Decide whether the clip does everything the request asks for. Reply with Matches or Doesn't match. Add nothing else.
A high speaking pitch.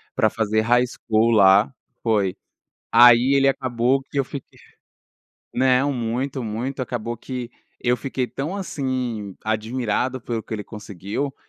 Doesn't match